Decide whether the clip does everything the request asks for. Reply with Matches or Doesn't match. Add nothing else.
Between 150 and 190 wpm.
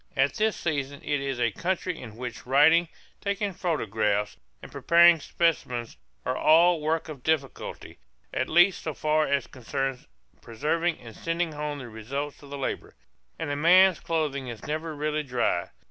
Matches